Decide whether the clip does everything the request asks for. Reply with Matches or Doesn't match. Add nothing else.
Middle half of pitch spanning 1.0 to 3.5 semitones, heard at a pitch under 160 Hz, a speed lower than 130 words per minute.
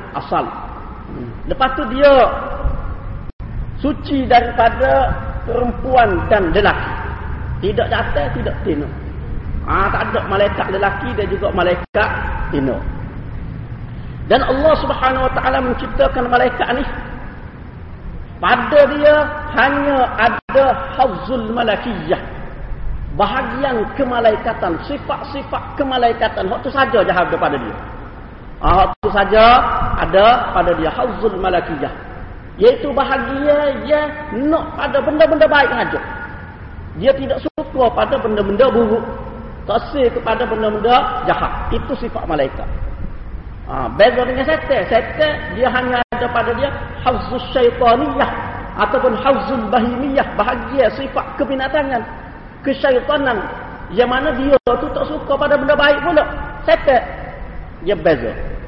Doesn't match